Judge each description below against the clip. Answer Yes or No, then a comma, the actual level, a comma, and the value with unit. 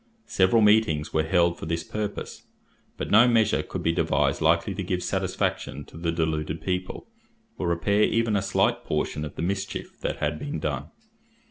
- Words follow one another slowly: No, average, 175 wpm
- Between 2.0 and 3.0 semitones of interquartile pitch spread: No, average, 4.3 semitones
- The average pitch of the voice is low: Yes, very low, 85 Hz